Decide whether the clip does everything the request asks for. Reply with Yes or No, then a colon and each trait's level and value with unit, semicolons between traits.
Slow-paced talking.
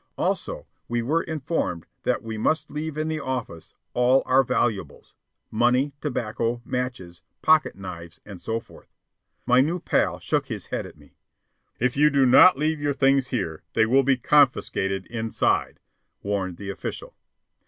No: average, 155 wpm